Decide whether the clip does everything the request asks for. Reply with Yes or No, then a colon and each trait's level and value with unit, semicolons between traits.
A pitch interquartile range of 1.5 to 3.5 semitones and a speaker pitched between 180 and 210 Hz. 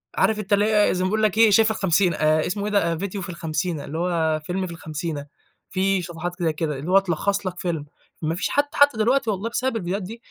No: average, 4.0 semitones; medium, 185 Hz